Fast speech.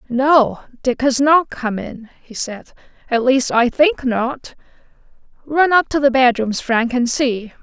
No: average, 165 wpm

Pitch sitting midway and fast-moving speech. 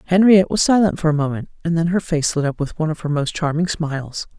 Yes: medium, 160 Hz; fast, 260 wpm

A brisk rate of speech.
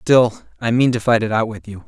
Yes: fast, 290 wpm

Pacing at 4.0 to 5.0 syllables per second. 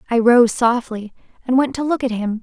No: 5.3 syllables/s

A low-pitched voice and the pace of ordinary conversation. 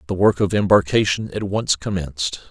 Yes: very low, 95 Hz; average, 170 wpm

